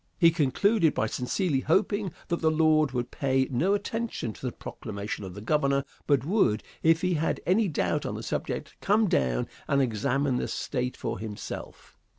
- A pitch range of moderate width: No, wide, 6.2 semitones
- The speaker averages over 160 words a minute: Yes, average, 175 wpm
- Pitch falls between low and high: Yes, medium, 145 Hz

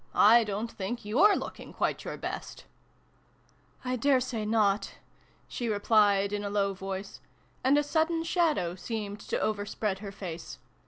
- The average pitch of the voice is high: Yes, high, 210 Hz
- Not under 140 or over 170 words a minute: Yes, average, 160 wpm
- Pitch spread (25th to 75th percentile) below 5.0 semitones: Yes, average, 3.8 semitones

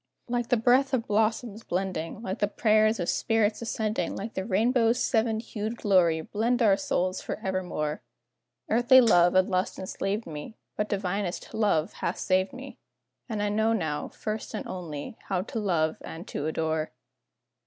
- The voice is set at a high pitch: Yes, high, 205 Hz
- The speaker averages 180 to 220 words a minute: No, average, 160 wpm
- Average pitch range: Yes, average, 3.5 semitones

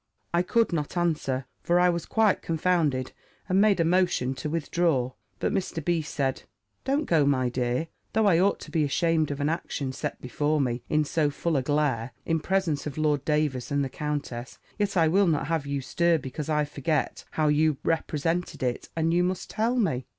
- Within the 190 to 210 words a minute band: Yes, average, 200 wpm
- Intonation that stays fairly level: No, average, 3.6 semitones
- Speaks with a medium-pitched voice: Yes, medium, 155 Hz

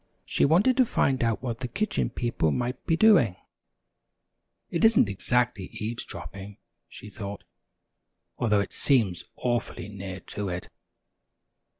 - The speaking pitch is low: Yes, low, 120 Hz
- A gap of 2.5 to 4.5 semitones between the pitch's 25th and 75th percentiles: No, average, 4.9 semitones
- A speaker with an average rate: No, slow, 125 wpm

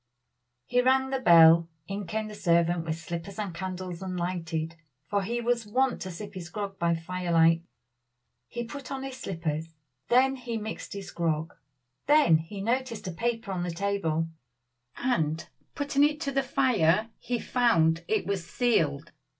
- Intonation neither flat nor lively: No, wide, 6.2 semitones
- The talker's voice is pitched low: No, high, 195 Hz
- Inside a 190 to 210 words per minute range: No, average, 165 wpm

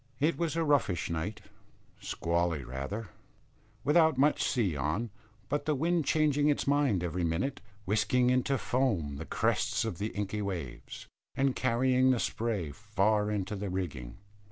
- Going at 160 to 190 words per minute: No, average, 150 wpm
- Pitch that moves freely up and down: Yes, wide, 7.6 semitones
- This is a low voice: Yes, low, 110 Hz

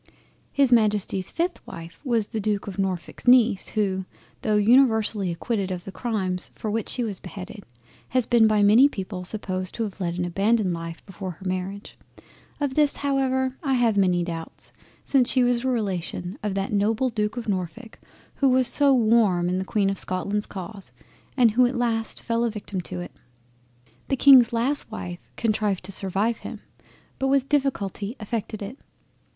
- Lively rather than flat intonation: No, average, 4.2 semitones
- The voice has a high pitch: Yes, high, 210 Hz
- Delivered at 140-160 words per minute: No, average, 175 wpm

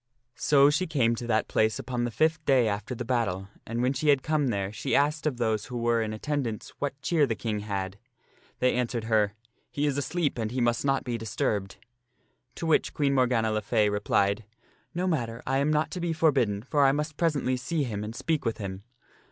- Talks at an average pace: No, fast, 225 wpm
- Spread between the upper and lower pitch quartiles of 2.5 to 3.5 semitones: No, average, 4.8 semitones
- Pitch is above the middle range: No, low, 125 Hz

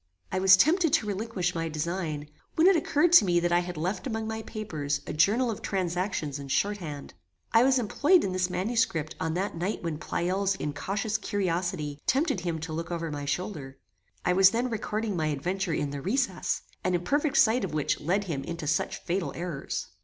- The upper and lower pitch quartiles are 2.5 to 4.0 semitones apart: No, average, 5.0 semitones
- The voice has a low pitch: No, medium, 185 Hz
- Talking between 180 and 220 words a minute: Yes, average, 195 wpm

